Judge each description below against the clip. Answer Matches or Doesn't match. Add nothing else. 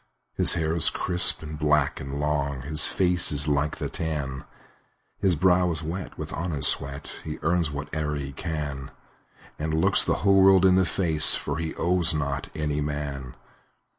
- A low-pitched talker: Matches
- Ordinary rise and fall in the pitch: Matches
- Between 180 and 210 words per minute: Doesn't match